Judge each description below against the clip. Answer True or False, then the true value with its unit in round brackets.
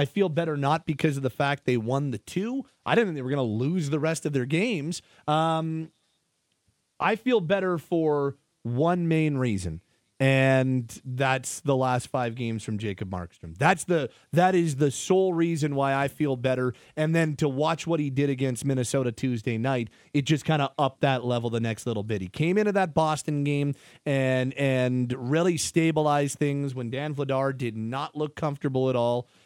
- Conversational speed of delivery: True (190 wpm)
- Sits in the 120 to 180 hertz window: True (140 Hz)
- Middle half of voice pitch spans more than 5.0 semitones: False (3.9 semitones)